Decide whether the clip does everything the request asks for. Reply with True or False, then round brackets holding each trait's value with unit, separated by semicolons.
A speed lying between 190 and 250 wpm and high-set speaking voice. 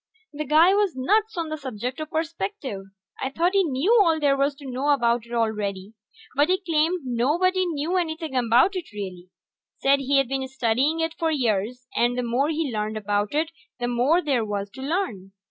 True (195 wpm; 275 Hz)